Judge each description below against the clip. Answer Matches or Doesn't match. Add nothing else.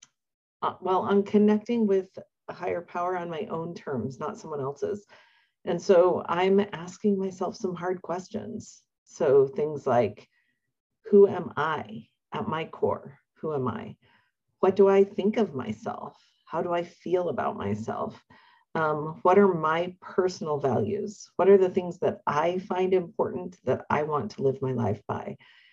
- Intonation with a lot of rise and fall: Doesn't match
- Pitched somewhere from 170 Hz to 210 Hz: Matches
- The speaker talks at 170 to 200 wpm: Doesn't match